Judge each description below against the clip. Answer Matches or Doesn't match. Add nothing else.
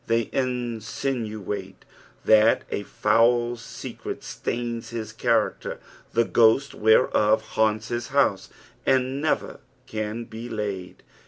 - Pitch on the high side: Doesn't match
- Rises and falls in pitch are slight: Matches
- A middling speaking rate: Doesn't match